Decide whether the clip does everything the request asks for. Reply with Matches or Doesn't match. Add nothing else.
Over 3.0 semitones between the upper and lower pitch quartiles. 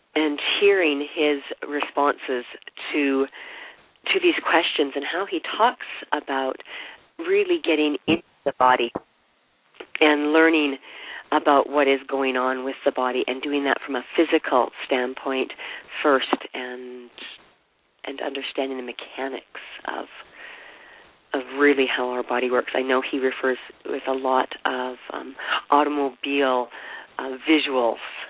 Doesn't match